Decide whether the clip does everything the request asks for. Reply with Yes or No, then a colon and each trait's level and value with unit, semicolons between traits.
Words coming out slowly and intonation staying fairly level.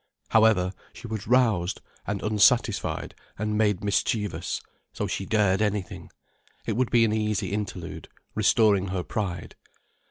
Yes: slow, 130 wpm; narrow, 2.1 semitones